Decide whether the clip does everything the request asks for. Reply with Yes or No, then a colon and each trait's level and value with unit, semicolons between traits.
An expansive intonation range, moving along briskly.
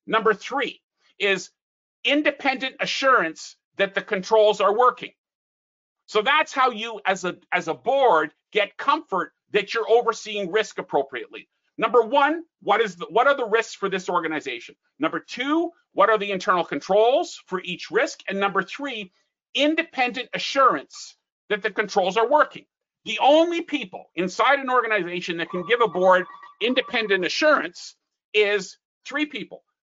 No: wide, 5.8 semitones; average, 150 wpm